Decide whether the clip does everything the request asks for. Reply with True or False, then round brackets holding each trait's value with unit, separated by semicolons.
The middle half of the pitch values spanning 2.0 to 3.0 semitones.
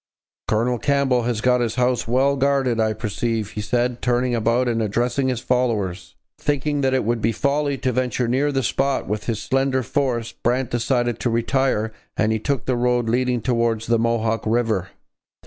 True (2.5 semitones)